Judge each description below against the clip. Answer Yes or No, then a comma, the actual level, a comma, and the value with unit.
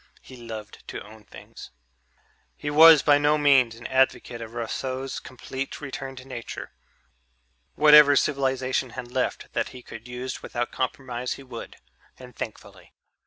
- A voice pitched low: Yes, low, 130 Hz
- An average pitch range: No, narrow, 2.2 semitones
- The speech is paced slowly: No, average, 145 wpm